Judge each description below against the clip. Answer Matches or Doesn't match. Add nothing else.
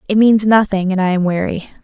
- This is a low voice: Doesn't match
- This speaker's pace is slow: Doesn't match